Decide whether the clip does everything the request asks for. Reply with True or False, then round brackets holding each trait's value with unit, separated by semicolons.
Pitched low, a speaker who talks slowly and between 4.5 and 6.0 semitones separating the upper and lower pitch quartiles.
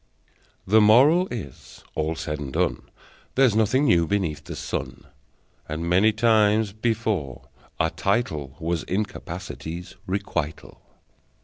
True (95 Hz; 115 wpm; 5.5 semitones)